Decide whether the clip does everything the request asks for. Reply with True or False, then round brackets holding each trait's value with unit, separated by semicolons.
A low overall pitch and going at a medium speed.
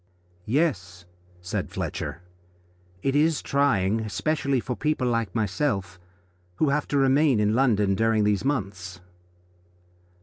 False (115 Hz; 115 wpm)